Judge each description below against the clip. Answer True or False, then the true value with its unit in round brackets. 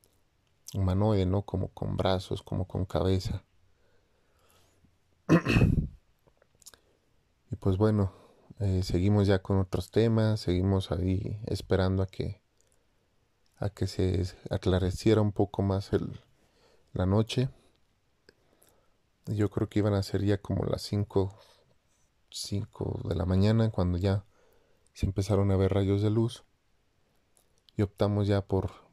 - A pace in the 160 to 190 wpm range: False (125 wpm)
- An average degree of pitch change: False (1.8 semitones)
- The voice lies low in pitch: True (100 Hz)